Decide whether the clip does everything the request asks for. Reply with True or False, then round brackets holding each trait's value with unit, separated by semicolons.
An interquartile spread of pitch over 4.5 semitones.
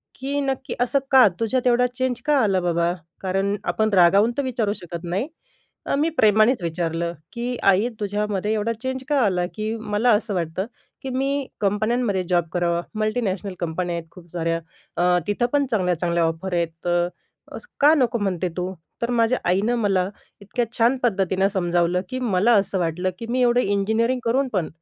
True (5.2 semitones)